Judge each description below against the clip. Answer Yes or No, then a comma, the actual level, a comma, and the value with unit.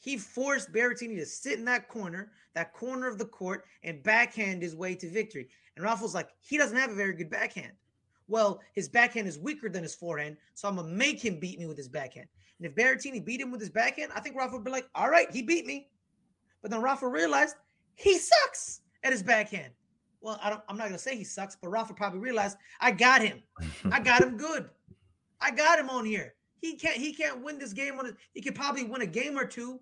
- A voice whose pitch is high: Yes, high, 225 Hz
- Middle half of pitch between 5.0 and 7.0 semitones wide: Yes, average, 5.3 semitones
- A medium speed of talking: No, fast, 235 wpm